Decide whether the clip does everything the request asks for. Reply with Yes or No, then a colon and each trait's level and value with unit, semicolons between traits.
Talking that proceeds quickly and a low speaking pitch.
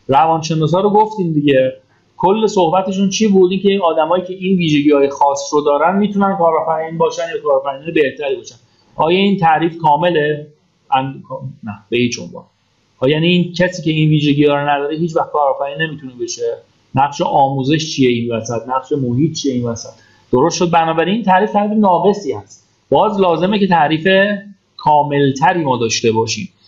No: fast, 165 wpm; medium, 155 Hz